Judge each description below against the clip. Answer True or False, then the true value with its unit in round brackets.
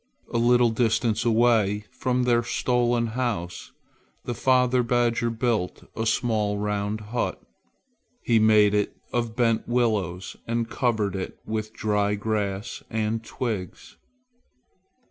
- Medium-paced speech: False (120 wpm)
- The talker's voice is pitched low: True (115 Hz)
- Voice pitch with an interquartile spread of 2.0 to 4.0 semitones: True (2.4 semitones)